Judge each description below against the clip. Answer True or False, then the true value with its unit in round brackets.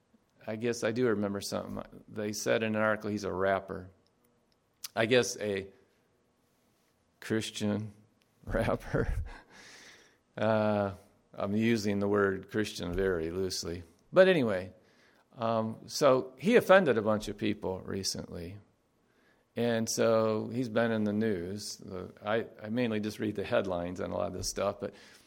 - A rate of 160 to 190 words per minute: False (145 wpm)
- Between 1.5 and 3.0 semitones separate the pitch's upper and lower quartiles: True (2.6 semitones)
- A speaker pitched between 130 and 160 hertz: False (105 Hz)